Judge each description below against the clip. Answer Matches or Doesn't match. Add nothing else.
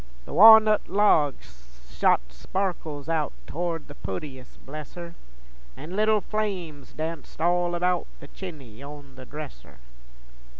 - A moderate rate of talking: Doesn't match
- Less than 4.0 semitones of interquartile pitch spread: Doesn't match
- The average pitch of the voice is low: Doesn't match